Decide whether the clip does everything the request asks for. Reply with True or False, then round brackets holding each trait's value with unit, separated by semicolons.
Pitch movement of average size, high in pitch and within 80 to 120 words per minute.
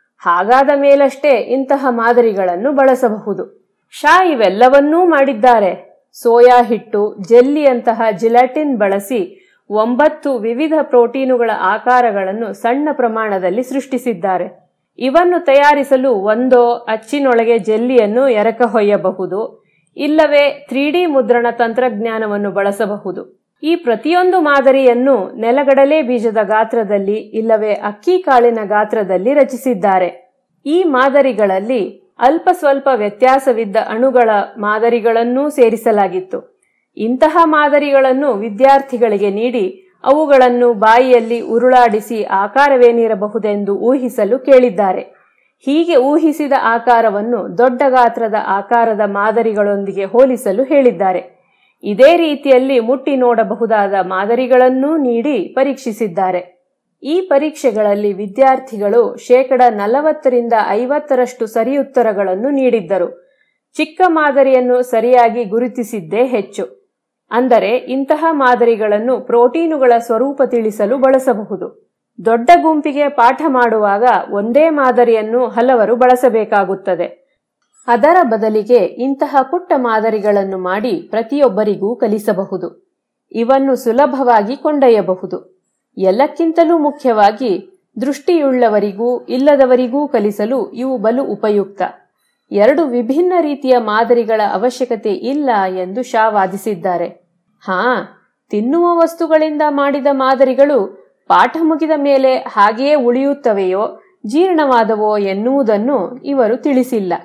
True (4.1 semitones; 245 Hz; 85 wpm)